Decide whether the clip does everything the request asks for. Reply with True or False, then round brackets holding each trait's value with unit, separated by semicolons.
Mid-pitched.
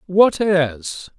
True (170 Hz)